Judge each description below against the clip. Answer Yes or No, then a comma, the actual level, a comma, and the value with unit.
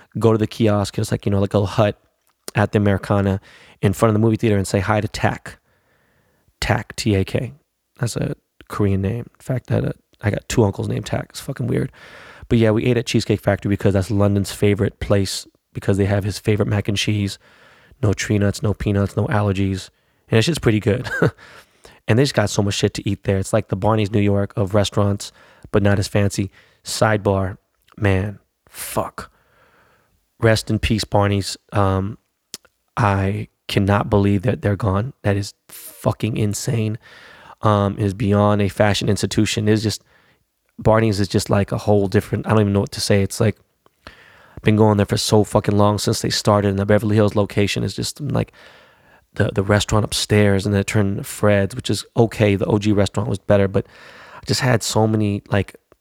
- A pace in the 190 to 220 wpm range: Yes, average, 200 wpm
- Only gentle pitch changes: Yes, narrow, 1.4 semitones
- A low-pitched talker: Yes, low, 105 Hz